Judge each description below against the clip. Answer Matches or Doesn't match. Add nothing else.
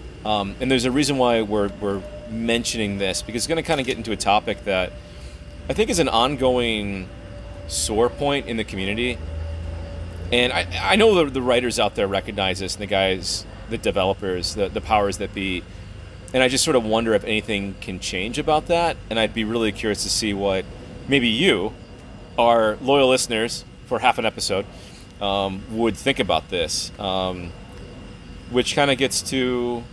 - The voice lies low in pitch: Matches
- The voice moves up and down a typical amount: Matches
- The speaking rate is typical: Matches